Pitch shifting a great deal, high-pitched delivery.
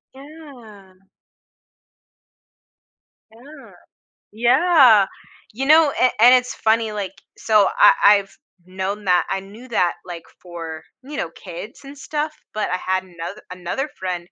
Yes: wide, 6.2 semitones; high, 210 Hz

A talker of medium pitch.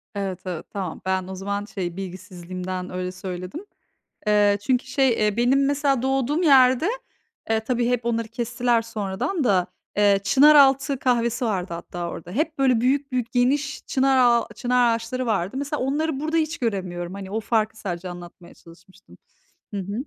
No: high, 230 Hz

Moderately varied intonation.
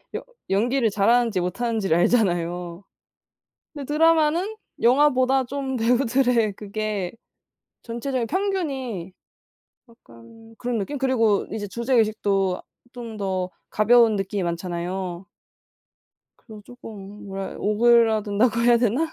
Yes: average, 4.1 semitones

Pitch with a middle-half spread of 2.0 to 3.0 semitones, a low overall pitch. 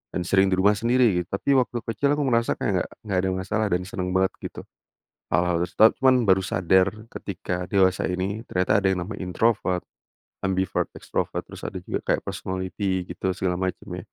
Yes: narrow, 2.5 semitones; very low, 95 Hz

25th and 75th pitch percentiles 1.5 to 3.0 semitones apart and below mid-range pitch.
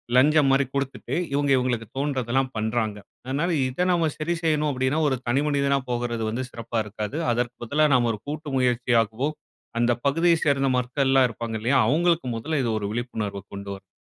No: average, 3.6 semitones; low, 130 Hz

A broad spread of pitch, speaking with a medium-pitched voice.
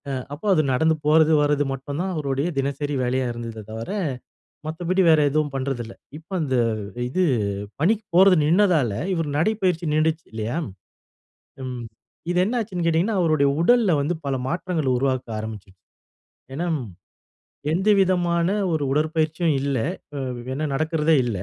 No: average, 4.3 semitones; medium, 155 Hz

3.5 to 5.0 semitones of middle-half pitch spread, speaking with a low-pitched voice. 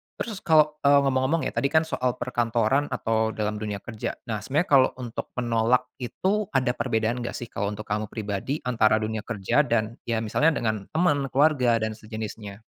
Yes: average, 4.3 semitones; low, 120 Hz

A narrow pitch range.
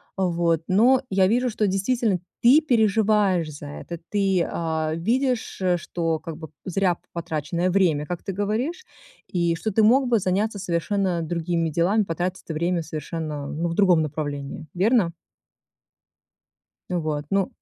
No: average, 4.1 semitones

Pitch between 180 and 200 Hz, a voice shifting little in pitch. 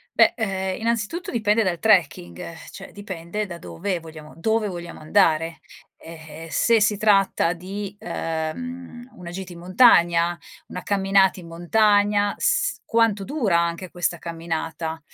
No: medium, 185 Hz; average, 3.9 semitones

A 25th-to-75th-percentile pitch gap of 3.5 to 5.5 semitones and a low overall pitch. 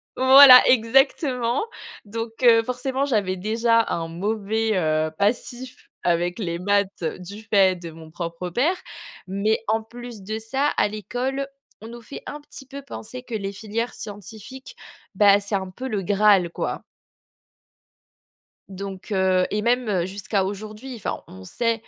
No: average, 4.2 semitones; high, 215 Hz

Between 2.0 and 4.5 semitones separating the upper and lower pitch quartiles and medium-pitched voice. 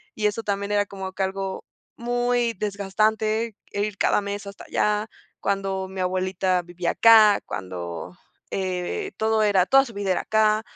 No: narrow, 2.4 semitones; high, 200 Hz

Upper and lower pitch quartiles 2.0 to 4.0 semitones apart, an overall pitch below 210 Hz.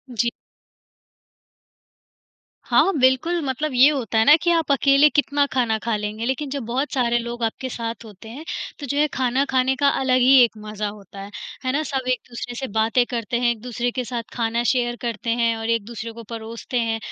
No: narrow, 2.6 semitones; high, 240 Hz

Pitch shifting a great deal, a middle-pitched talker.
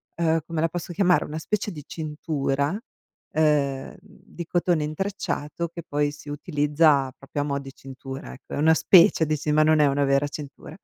No: narrow, 2.5 semitones; medium, 150 Hz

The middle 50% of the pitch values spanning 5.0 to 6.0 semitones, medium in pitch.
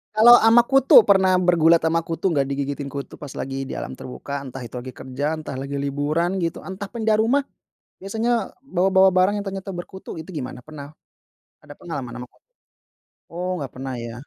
Yes: wide, 5.6 semitones; medium, 160 Hz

